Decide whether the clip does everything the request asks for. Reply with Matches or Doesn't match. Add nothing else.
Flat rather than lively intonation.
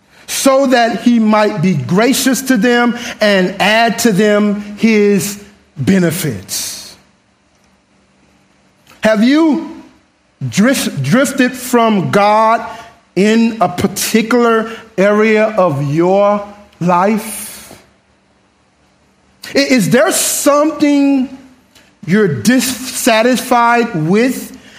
Doesn't match